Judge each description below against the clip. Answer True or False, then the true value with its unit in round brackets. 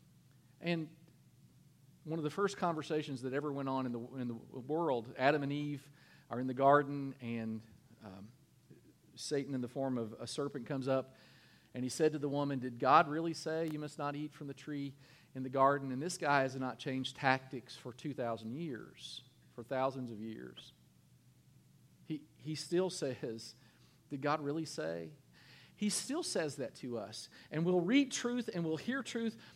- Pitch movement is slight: False (3.4 semitones)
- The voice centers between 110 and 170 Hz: True (140 Hz)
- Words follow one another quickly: False (180 wpm)